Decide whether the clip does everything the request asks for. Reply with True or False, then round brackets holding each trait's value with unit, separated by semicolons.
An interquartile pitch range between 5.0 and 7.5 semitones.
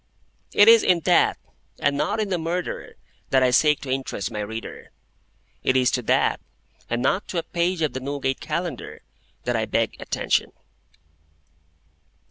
True (5.3 semitones)